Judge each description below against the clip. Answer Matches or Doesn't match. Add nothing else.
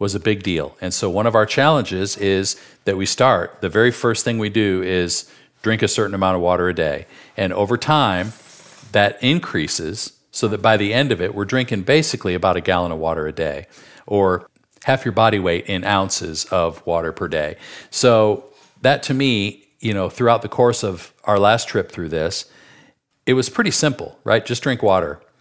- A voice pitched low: Matches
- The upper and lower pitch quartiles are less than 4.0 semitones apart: Doesn't match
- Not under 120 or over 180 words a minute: Doesn't match